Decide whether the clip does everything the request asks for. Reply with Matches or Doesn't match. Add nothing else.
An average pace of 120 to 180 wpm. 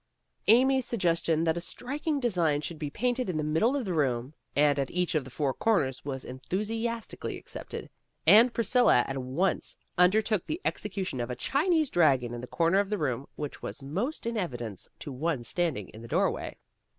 Doesn't match